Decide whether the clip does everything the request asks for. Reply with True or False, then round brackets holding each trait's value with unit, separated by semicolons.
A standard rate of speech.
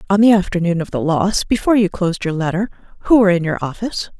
False (230 wpm)